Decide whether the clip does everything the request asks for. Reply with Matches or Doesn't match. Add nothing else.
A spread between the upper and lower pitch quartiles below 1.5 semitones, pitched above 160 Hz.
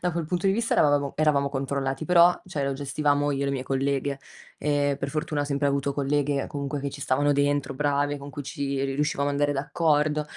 Doesn't match